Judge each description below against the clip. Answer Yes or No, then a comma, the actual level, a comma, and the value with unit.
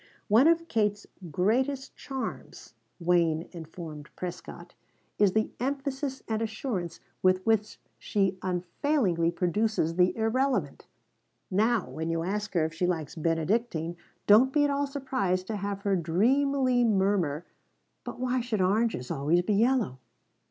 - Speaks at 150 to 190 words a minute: No, slow, 135 wpm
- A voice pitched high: Yes, high, 205 Hz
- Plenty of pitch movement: Yes, wide, 6.2 semitones